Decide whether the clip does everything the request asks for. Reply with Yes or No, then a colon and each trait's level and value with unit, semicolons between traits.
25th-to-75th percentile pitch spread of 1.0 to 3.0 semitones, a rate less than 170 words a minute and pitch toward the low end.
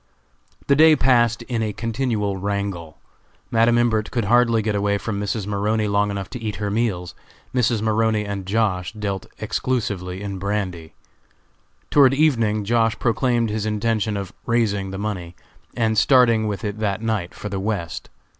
Yes: narrow, 2.5 semitones; average, 160 wpm; low, 105 Hz